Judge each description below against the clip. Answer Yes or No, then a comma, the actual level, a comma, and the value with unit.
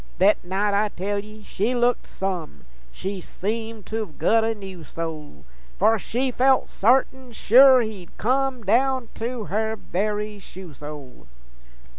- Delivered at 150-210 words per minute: No, average, 140 wpm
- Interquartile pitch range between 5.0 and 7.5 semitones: No, average, 3.8 semitones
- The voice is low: No, high, 210 Hz